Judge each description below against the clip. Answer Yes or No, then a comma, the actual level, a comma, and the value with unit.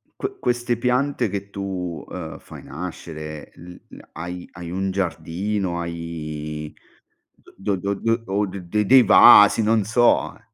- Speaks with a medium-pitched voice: No, very low, 95 Hz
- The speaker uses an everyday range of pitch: Yes, average, 4.1 semitones